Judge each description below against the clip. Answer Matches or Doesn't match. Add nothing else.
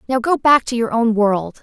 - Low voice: Doesn't match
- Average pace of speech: Doesn't match